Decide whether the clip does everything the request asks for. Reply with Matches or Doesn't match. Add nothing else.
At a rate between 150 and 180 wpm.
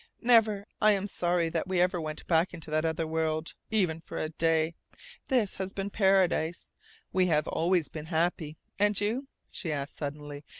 Matches